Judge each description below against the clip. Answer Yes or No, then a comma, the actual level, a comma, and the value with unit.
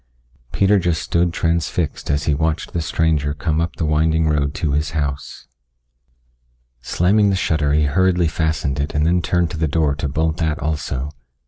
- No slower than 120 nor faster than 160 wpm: No, average, 180 wpm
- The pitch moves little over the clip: Yes, narrow, 2.3 semitones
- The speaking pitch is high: No, very low, 80 Hz